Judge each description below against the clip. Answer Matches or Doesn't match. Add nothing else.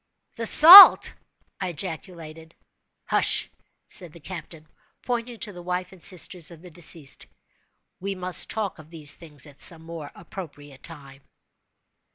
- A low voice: Doesn't match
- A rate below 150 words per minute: Matches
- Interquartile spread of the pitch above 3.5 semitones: Doesn't match